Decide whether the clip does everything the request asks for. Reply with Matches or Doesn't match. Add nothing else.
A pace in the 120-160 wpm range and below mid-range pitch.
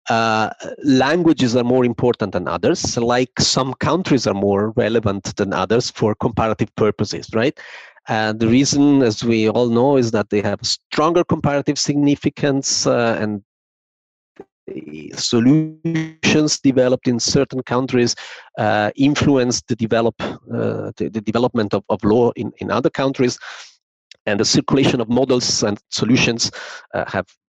Matches